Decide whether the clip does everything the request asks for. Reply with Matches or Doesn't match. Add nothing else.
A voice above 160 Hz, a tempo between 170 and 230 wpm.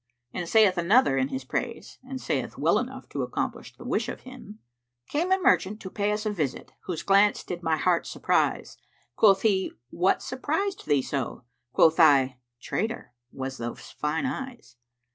Matches